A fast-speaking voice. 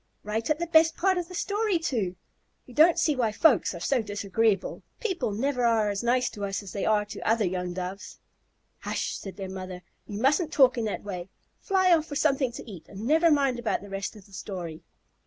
Yes: fast, 225 wpm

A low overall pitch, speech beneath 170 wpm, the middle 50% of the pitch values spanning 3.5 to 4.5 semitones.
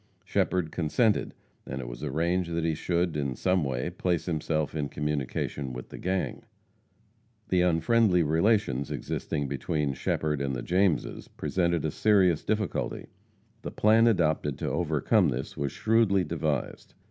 Yes: very low, 80 Hz; average, 145 wpm; average, 4.2 semitones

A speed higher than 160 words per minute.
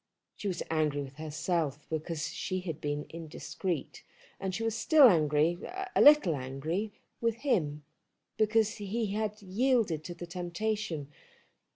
No: average, 140 wpm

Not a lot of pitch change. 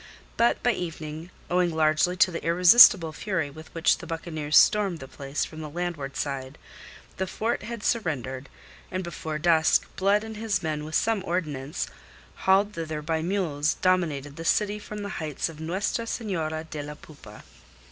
No: average, 3.9 semitones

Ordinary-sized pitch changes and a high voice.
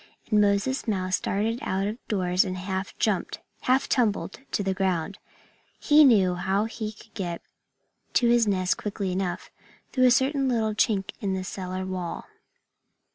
Yes: average, 3.3 semitones; high, 200 Hz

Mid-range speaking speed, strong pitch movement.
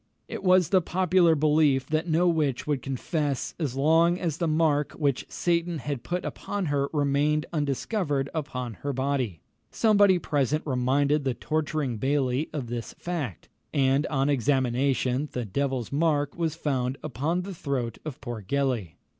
No: average, 155 wpm; average, 3.3 semitones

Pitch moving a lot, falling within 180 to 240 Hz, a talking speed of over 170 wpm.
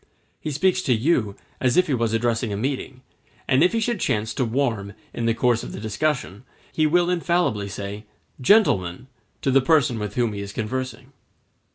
No: wide, 5.9 semitones; low, 125 Hz; average, 190 wpm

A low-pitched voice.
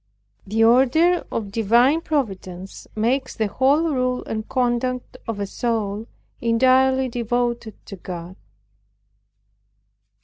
No: high, 240 Hz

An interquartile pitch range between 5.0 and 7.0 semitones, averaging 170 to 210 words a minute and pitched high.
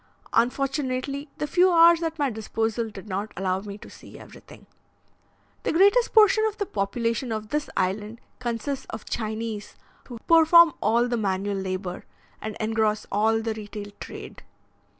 No: wide, 5.5 semitones; average, 150 wpm; high, 225 Hz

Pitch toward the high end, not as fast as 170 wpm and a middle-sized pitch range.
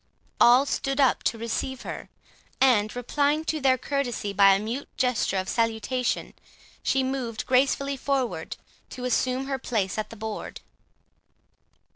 Yes: very high, 250 Hz; average, 140 wpm; average, 3.3 semitones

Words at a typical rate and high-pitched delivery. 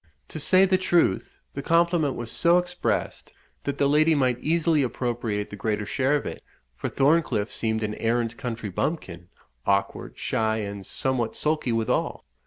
No: average, 160 wpm; low, 125 Hz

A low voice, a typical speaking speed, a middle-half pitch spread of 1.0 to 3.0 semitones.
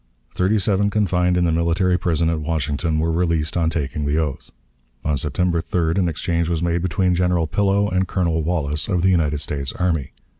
Yes: very low, 85 Hz; average, 190 wpm; narrow, 2.6 semitones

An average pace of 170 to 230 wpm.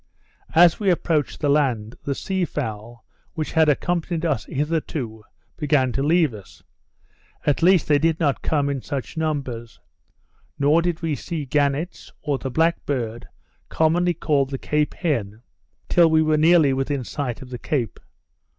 No: average, 160 wpm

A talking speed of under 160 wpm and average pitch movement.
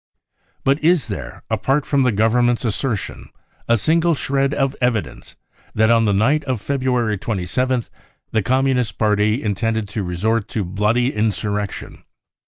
Yes: average, 150 wpm; average, 3.9 semitones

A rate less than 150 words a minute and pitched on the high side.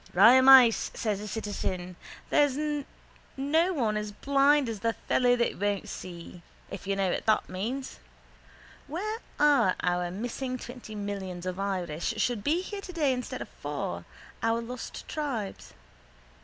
Yes: average, 140 wpm; high, 230 Hz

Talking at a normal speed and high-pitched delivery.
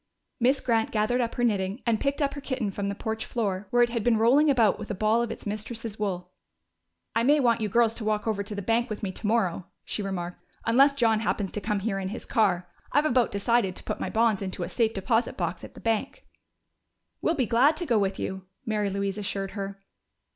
No: fast, 235 wpm; high, 220 Hz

